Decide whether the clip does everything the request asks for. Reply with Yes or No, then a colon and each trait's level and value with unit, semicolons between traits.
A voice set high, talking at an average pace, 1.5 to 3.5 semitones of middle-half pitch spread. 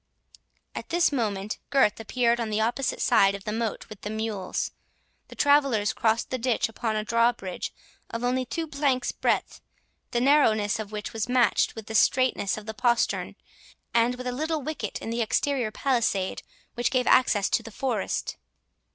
Yes: high, 230 Hz; average, 175 wpm; average, 3.0 semitones